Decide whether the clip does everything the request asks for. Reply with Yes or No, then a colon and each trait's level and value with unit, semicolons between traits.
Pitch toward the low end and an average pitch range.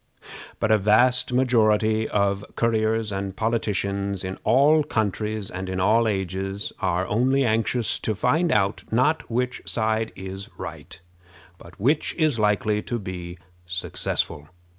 Yes: low, 110 Hz; average, 3.1 semitones